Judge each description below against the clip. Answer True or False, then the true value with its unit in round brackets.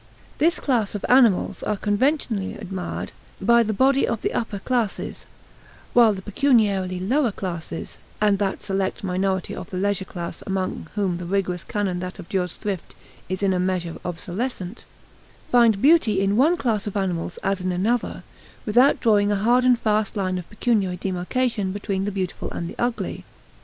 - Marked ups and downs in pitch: False (3.7 semitones)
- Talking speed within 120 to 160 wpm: False (170 wpm)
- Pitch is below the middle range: False (200 Hz)